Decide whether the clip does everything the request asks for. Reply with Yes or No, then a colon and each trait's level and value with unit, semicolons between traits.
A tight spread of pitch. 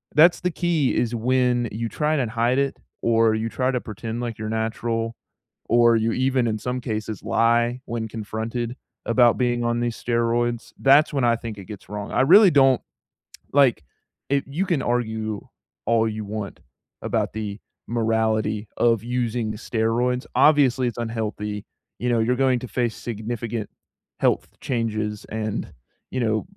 Yes: narrow, 2.1 semitones